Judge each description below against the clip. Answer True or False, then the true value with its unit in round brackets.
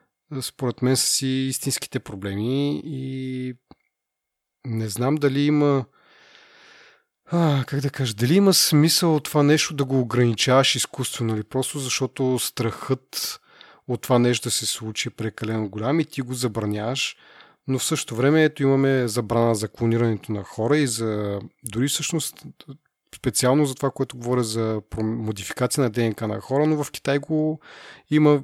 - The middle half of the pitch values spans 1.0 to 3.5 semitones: False (3.9 semitones)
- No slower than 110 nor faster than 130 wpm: False (155 wpm)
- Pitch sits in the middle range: False (130 Hz)